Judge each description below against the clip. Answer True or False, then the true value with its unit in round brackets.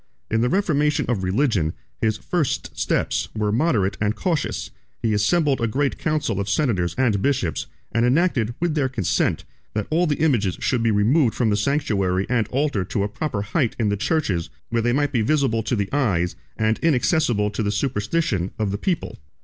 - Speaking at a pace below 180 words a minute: False (190 wpm)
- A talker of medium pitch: False (115 Hz)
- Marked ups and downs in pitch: True (5.9 semitones)